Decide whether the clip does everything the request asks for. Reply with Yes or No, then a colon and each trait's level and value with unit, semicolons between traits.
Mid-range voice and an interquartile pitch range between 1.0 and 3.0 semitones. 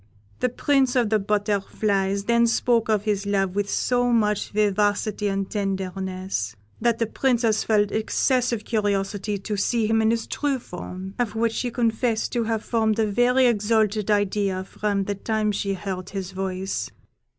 No: high, 210 Hz; average, 2.7 semitones